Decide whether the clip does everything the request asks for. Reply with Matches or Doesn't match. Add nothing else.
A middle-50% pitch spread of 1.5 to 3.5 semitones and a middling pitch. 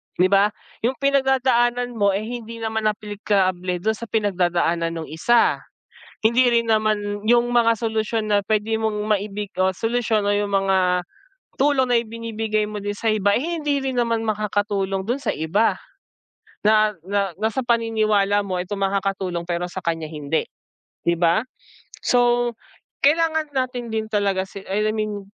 Doesn't match